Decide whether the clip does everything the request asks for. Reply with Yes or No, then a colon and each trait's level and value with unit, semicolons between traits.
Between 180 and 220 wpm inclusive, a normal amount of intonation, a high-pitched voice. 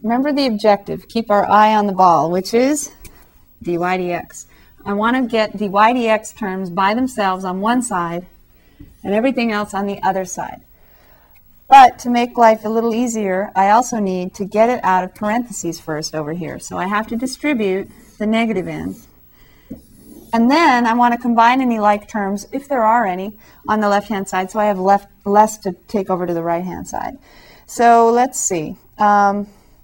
Yes: average, 190 wpm; average, 3.5 semitones; high, 210 Hz